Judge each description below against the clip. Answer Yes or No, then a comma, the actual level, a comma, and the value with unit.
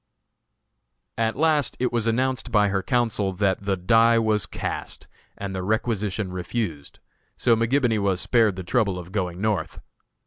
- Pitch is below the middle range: Yes, low, 105 Hz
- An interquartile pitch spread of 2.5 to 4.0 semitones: Yes, average, 3.5 semitones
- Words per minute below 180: Yes, average, 150 wpm